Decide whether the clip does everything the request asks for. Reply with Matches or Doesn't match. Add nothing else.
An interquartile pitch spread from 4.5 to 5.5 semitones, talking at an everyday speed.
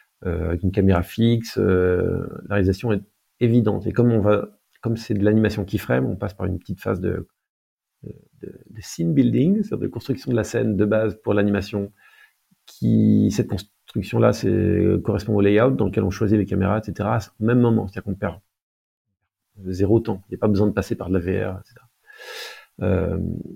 Doesn't match